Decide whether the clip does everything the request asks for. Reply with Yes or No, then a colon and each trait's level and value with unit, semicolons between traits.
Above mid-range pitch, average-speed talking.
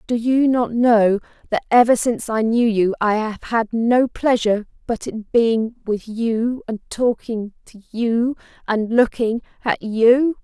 Yes: high, 230 Hz; average, 160 wpm